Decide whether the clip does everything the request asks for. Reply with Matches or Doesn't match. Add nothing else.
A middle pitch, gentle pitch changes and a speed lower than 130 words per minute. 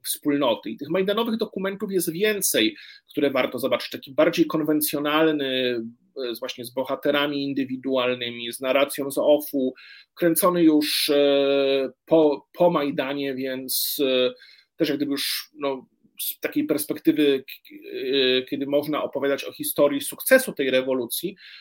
Doesn't match